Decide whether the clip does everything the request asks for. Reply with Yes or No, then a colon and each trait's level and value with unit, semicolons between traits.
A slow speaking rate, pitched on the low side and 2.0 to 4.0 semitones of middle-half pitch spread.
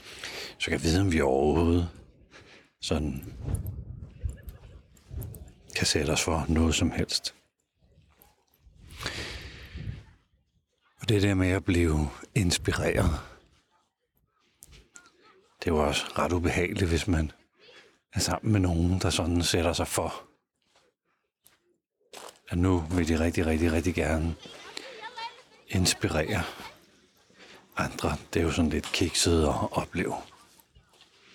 Yes: slow, 105 wpm; very low, 85 Hz; narrow, 2.5 semitones